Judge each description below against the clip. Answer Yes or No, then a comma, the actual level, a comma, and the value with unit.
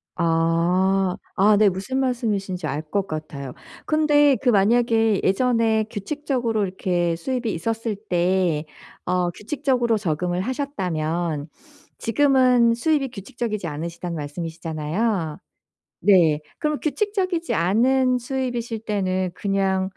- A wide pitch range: Yes, wide, 5.9 semitones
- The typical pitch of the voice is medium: No, high, 200 Hz